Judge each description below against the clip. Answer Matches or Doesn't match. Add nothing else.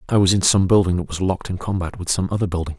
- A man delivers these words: Matches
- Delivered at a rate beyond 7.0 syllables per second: Matches